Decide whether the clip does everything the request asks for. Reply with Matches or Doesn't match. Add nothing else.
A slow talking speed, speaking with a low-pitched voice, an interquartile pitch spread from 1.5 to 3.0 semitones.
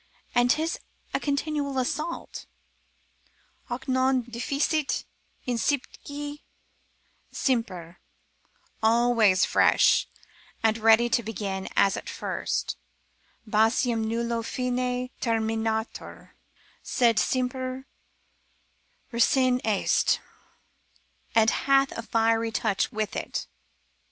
Doesn't match